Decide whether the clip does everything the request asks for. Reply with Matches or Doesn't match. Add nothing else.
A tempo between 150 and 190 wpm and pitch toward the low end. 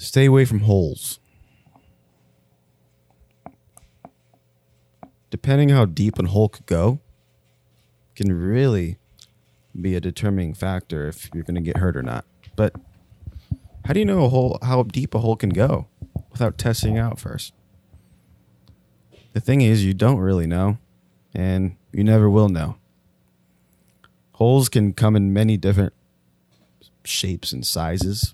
Doesn't match